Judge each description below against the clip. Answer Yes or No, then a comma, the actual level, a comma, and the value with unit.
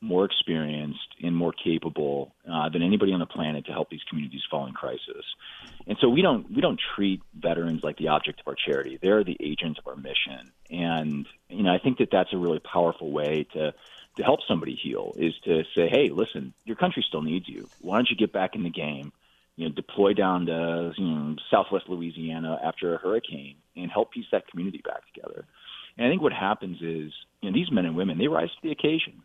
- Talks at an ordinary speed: No, fast, 220 wpm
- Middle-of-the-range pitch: No, very low, 80 Hz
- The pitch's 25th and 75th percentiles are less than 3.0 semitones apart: Yes, narrow, 2.5 semitones